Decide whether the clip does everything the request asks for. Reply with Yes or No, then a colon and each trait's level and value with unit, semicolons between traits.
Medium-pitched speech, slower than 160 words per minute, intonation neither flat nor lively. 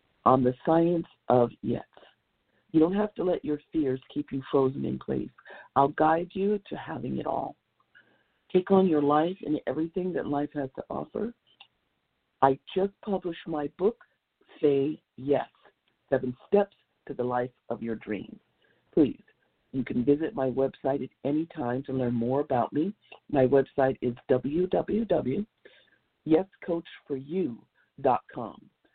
Yes: medium, 145 Hz; average, 140 wpm; average, 4.4 semitones